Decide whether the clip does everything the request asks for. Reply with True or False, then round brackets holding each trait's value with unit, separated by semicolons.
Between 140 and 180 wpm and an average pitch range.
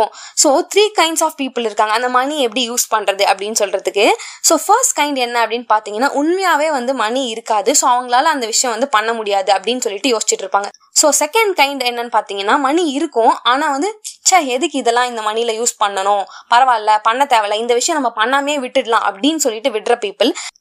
True (165 wpm; 5.0 semitones)